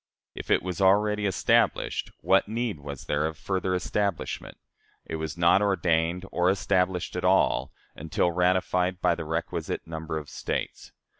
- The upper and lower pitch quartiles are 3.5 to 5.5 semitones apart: No, average, 3.0 semitones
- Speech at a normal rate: Yes, average, 150 wpm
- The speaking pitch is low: Yes, very low, 90 Hz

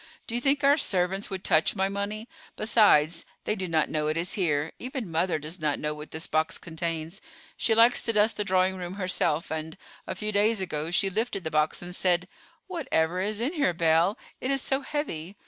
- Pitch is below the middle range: No, medium, 185 Hz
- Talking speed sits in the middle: No, fast, 210 wpm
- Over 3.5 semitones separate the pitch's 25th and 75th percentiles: Yes, average, 4.9 semitones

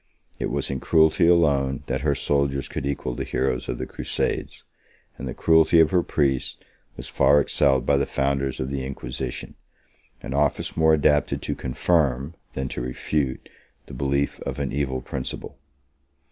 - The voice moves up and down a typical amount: No, narrow, 1.8 semitones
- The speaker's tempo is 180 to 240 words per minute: No, average, 170 wpm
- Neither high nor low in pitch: No, very low, 70 Hz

